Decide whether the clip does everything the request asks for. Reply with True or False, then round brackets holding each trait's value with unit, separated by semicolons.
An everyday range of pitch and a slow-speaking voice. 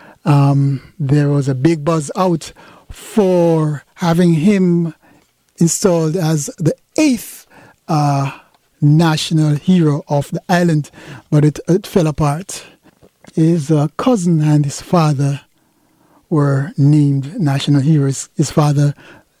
True (3.0 semitones; 115 wpm)